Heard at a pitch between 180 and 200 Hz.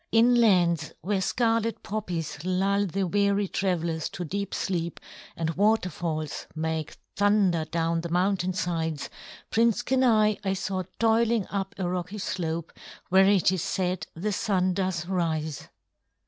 Yes: medium, 185 Hz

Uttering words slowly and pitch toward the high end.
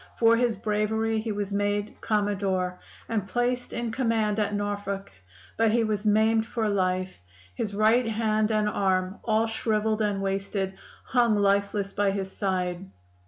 No: average, 150 wpm; high, 210 Hz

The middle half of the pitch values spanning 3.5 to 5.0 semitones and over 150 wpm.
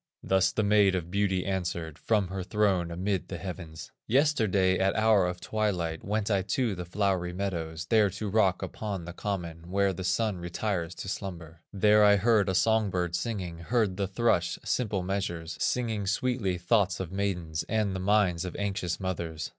No: average, 2.9 semitones; average, 180 wpm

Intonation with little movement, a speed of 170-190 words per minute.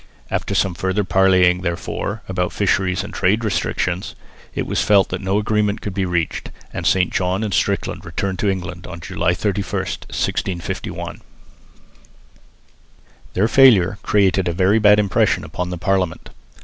No: narrow, 2.2 semitones; average, 150 wpm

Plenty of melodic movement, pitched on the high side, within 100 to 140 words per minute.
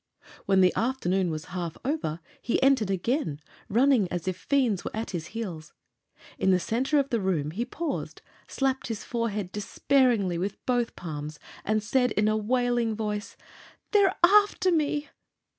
No: wide, 6.1 semitones; high, 215 Hz; average, 160 wpm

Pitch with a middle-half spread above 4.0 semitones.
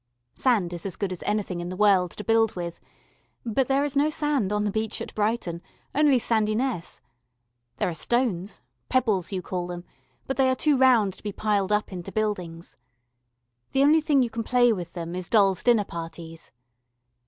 Yes: wide, 5.5 semitones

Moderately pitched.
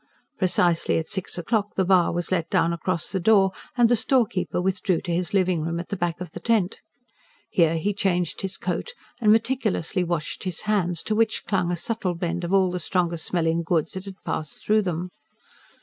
Yes: medium, 180 Hz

